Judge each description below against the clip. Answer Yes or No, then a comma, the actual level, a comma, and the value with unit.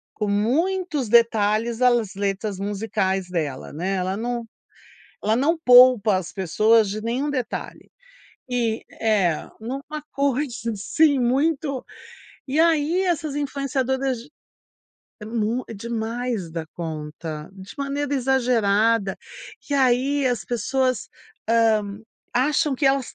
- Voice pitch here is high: Yes, high, 235 Hz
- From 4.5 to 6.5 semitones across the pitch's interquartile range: Yes, average, 4.9 semitones